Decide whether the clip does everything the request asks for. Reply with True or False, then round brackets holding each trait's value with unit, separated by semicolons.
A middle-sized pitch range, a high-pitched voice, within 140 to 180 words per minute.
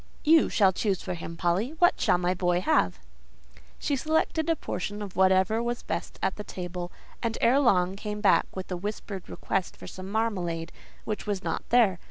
False (4.1 semitones; 195 Hz; 190 wpm)